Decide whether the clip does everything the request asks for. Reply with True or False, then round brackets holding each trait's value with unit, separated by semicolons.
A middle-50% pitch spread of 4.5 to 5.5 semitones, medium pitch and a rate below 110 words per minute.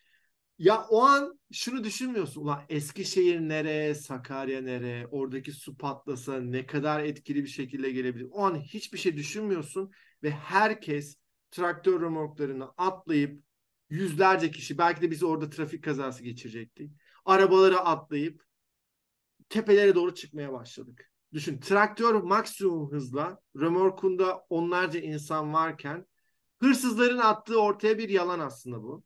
False (4.8 semitones; 160 Hz; 120 wpm)